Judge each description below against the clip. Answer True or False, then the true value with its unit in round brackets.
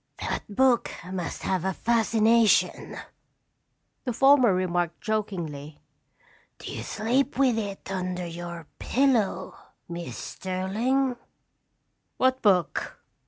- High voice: True (205 Hz)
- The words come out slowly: True (100 wpm)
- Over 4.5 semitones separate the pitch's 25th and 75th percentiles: True (5.1 semitones)